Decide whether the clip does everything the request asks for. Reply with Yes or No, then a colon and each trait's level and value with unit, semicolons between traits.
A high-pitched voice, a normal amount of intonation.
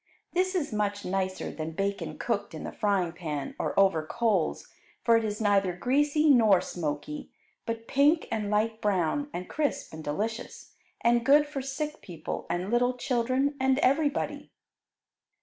No: high, 220 Hz; wide, 6.4 semitones